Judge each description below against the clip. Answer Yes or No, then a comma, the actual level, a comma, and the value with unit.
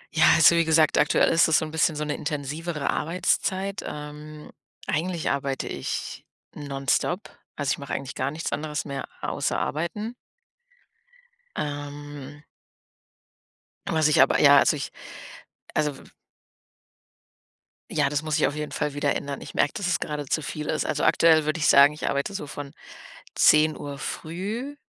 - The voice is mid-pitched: Yes, medium, 150 Hz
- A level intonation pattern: Yes, narrow, 2.0 semitones